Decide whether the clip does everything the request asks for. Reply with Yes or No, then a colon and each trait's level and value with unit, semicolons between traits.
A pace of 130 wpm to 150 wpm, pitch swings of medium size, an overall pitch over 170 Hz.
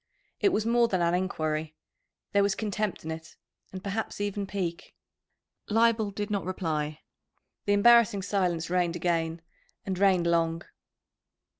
Yes: average, 140 wpm; average, 3.4 semitones; medium, 185 Hz